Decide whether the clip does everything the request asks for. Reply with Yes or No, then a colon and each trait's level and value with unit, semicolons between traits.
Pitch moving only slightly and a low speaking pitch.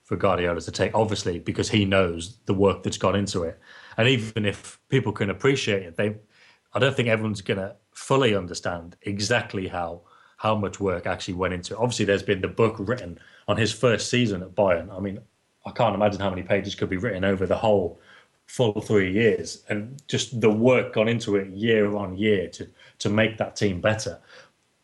Yes: narrow, 2.3 semitones; low, 105 Hz